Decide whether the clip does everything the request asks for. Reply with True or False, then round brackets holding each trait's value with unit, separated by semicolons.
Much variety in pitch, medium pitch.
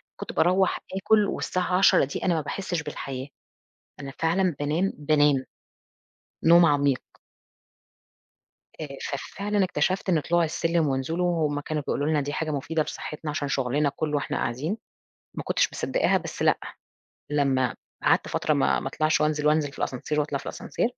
False (3.2 semitones; 150 Hz)